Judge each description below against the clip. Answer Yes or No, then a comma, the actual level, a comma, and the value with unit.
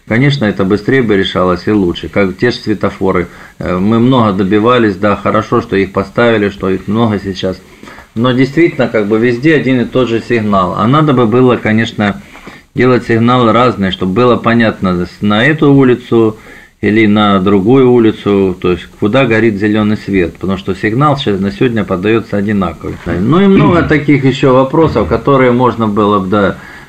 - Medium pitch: No, low, 110 Hz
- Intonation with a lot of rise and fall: No, average, 3.8 semitones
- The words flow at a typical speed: No, fast, 170 wpm